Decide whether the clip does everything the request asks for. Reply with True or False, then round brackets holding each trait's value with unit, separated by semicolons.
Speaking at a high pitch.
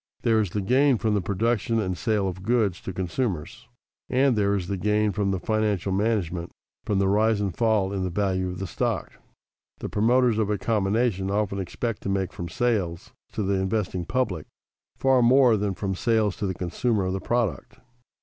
False (100 Hz)